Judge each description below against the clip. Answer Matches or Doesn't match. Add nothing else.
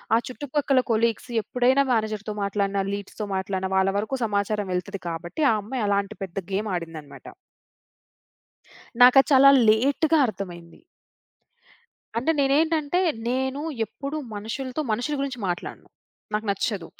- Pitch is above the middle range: Matches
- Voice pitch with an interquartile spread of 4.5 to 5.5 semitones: Matches